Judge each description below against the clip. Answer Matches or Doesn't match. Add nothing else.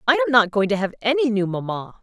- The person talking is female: Matches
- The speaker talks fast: Matches